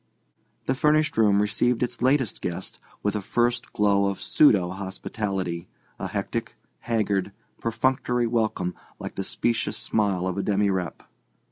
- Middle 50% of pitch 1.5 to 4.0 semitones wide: Yes, average, 3.5 semitones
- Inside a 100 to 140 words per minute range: Yes, slow, 135 wpm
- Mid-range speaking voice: No, low, 105 Hz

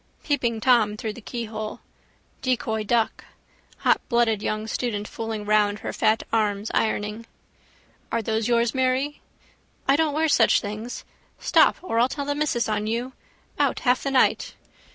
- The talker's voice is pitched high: Yes, high, 230 Hz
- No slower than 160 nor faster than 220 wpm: No, average, 150 wpm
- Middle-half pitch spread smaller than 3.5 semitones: Yes, average, 3.0 semitones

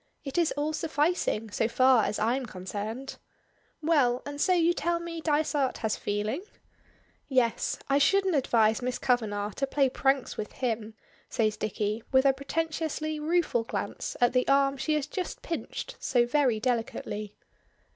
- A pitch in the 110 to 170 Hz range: No, very high, 265 Hz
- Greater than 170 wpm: No, average, 155 wpm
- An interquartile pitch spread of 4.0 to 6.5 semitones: Yes, average, 5.3 semitones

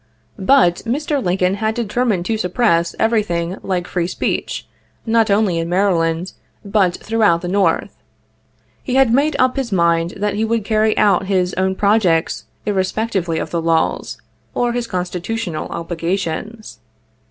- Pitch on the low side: No, high, 195 Hz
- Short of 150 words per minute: Yes, average, 140 wpm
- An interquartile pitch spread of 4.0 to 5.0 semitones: Yes, average, 4.3 semitones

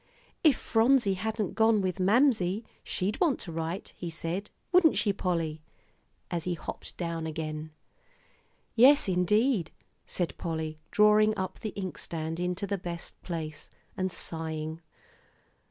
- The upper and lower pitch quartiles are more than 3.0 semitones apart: Yes, average, 4.5 semitones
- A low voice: No, medium, 185 Hz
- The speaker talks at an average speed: No, slow, 130 wpm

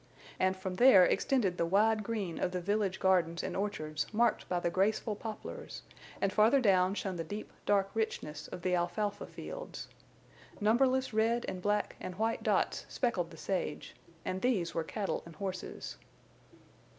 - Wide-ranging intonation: No, average, 3.3 semitones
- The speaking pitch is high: Yes, high, 195 Hz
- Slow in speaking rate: No, average, 165 wpm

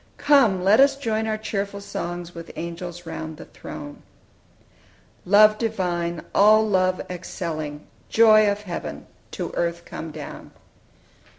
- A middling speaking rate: No, slow, 125 wpm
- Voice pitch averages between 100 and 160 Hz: No, medium, 185 Hz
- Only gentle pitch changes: No, average, 4.1 semitones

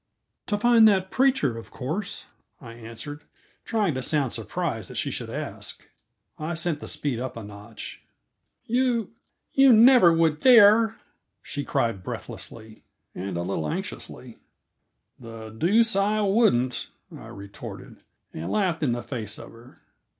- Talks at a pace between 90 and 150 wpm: Yes, average, 145 wpm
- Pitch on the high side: No, medium, 150 Hz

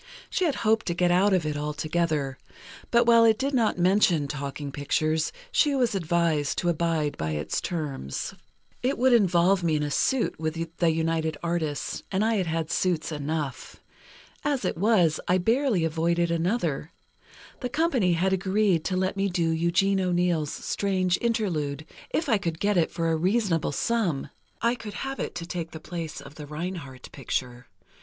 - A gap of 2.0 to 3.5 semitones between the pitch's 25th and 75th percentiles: No, average, 4.6 semitones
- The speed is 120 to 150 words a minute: No, average, 175 wpm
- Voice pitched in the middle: Yes, medium, 170 Hz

